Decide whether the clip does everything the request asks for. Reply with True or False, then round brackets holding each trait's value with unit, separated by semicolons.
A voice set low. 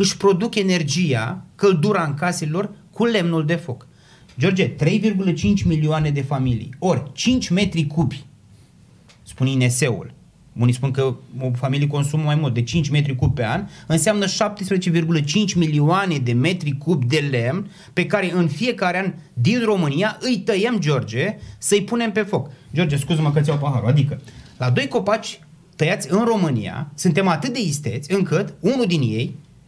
False (160 Hz)